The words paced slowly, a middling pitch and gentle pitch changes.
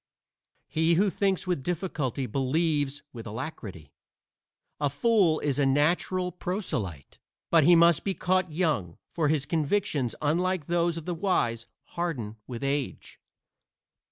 No: slow, 130 wpm; medium, 155 Hz; average, 4.8 semitones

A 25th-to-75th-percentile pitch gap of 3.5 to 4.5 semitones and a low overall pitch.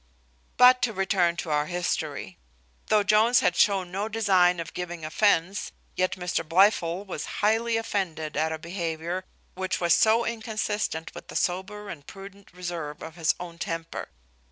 No: average, 3.8 semitones; medium, 180 Hz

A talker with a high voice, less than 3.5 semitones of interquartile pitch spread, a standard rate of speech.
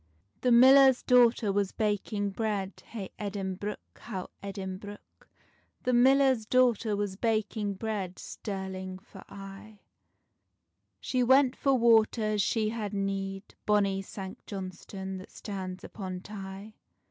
No: high, 205 Hz; average, 2.7 semitones; slow, 120 wpm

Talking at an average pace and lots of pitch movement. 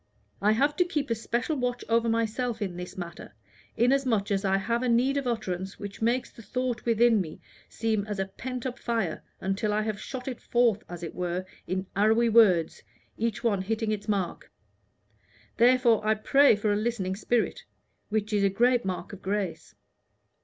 No: average, 180 wpm; average, 3.4 semitones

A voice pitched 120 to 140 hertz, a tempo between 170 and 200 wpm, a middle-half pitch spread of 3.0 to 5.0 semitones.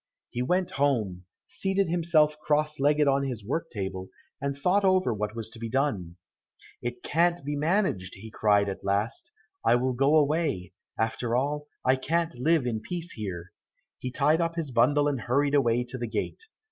No: low, 135 Hz; average, 180 wpm; wide, 5.4 semitones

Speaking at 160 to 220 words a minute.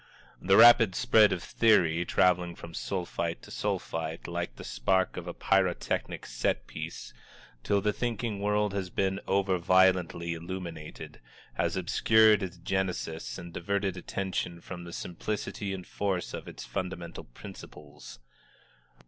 No: average, 140 wpm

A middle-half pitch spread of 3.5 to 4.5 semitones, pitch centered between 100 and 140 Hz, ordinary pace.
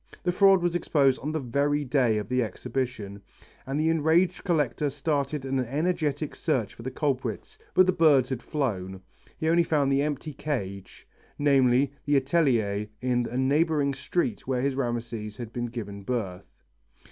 Yes: average, 4.0 semitones; low, 135 Hz; average, 165 wpm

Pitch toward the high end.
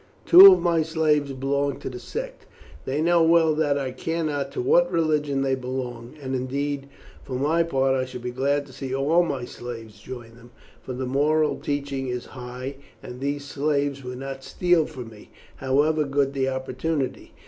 No: low, 135 Hz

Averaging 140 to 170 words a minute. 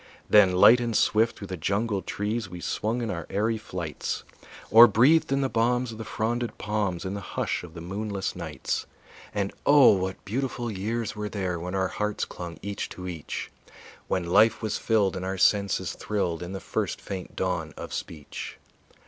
No: average, 185 wpm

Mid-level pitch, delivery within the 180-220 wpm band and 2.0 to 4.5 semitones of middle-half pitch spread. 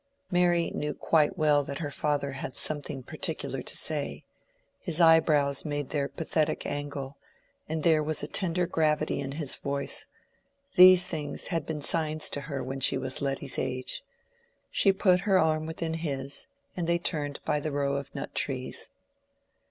No: medium, 150 Hz; average, 165 wpm; narrow, 2.6 semitones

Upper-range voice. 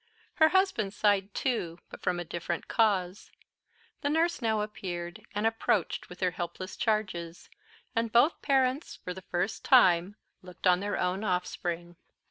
Yes: high, 195 Hz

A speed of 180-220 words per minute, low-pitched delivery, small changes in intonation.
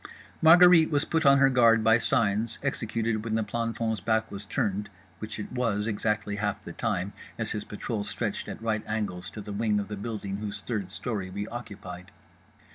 Yes: average, 190 wpm; low, 110 Hz; narrow, 2.2 semitones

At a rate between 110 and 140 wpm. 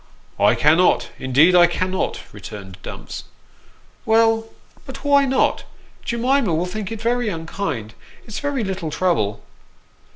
Yes: slow, 135 wpm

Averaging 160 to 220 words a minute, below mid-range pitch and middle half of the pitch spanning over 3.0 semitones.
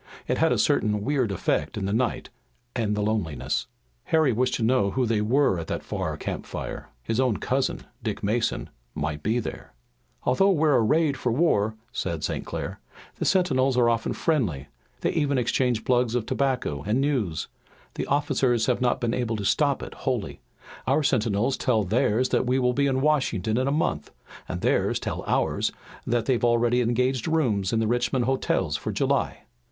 Yes: average, 180 wpm; low, 120 Hz; average, 3.7 semitones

